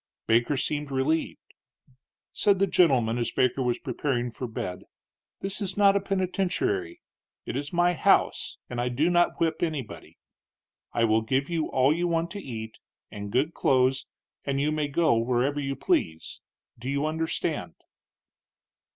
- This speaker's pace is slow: No, average, 155 wpm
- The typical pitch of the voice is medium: Yes, medium, 145 Hz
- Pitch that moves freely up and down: Yes, wide, 5.8 semitones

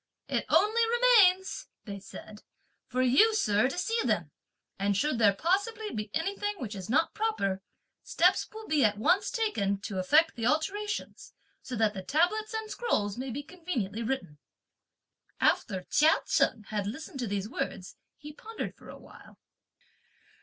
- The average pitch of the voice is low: No, very high, 285 Hz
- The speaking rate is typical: Yes, average, 160 wpm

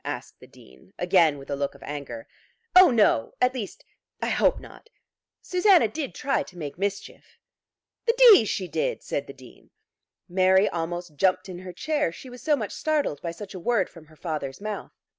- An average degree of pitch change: No, wide, 8.0 semitones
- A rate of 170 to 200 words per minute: Yes, average, 190 wpm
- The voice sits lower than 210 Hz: Yes, medium, 185 Hz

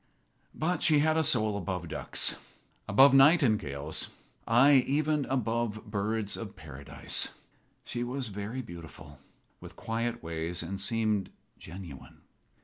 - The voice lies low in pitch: Yes, low, 110 Hz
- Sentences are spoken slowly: Yes, slow, 120 wpm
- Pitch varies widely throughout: Yes, wide, 6.5 semitones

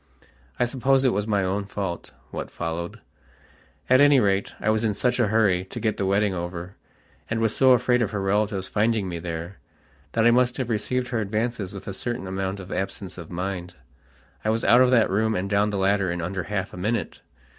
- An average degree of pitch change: Yes, average, 3.5 semitones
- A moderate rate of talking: No, fast, 215 wpm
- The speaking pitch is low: Yes, low, 105 Hz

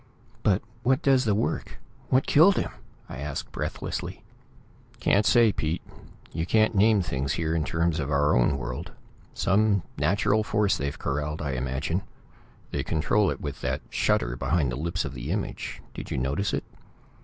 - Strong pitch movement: Yes, wide, 6.8 semitones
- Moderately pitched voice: No, very low, 80 Hz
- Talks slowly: No, average, 165 wpm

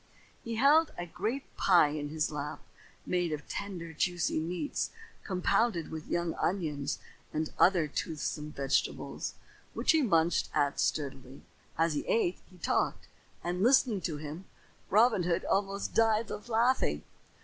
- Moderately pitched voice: Yes, medium, 175 Hz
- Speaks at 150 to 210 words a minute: No, average, 140 wpm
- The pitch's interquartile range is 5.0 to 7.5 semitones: Yes, average, 5.3 semitones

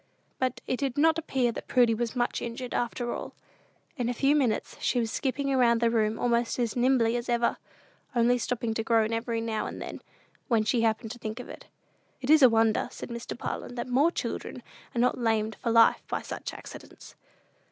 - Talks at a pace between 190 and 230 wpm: Yes, fast, 205 wpm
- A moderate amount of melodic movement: No, narrow, 1.8 semitones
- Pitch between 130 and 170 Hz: No, high, 240 Hz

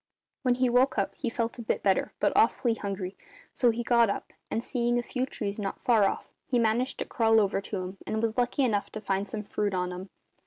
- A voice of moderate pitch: No, high, 225 Hz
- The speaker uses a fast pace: Yes, fast, 235 wpm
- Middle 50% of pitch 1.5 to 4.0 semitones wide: Yes, average, 3.3 semitones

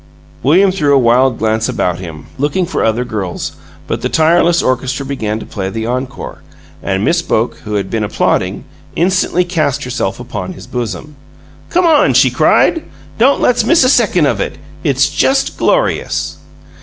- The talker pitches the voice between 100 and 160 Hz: Yes, low, 135 Hz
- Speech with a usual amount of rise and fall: No, wide, 7.8 semitones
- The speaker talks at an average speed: Yes, average, 170 wpm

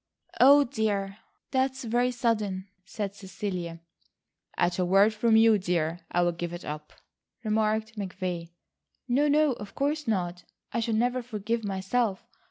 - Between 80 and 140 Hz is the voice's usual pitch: No, high, 210 Hz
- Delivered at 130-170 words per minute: Yes, average, 140 wpm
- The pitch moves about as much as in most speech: Yes, average, 4.3 semitones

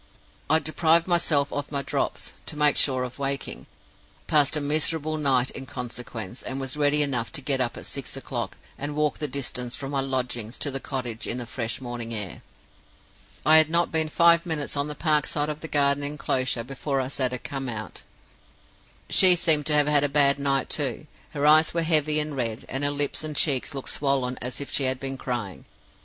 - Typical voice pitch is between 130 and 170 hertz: Yes, medium, 140 Hz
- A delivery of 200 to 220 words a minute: Yes, fast, 205 wpm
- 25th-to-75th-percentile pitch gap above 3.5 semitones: No, average, 2.7 semitones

